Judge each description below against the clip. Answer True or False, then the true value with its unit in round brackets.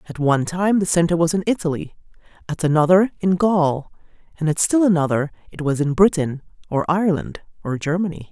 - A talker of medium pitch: True (170 Hz)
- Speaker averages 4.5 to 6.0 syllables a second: True (5.8 syllables/s)